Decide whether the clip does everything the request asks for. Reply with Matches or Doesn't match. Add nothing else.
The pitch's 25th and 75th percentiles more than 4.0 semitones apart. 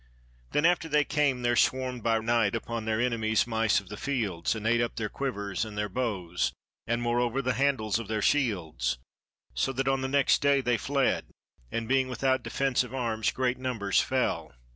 Doesn't match